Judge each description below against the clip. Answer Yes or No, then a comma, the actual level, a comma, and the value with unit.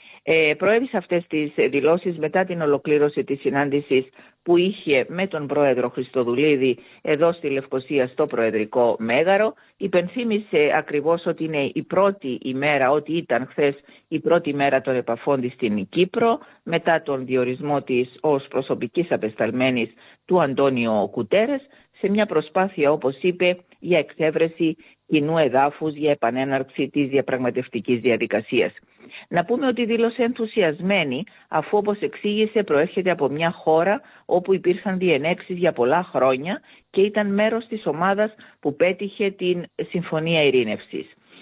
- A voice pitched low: No, medium, 160 Hz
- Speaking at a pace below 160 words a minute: Yes, average, 130 wpm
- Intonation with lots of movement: Yes, wide, 5.7 semitones